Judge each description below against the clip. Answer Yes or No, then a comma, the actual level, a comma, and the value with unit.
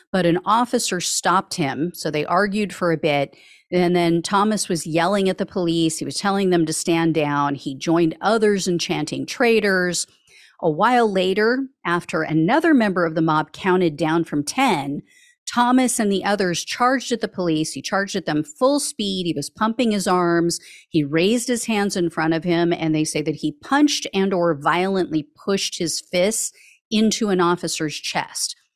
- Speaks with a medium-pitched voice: Yes, medium, 180 Hz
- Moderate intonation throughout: Yes, average, 4.1 semitones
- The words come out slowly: No, average, 185 wpm